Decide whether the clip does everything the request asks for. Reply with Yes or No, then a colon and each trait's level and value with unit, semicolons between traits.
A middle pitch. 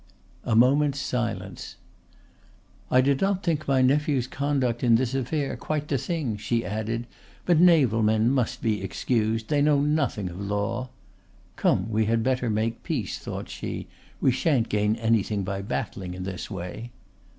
No: low, 120 Hz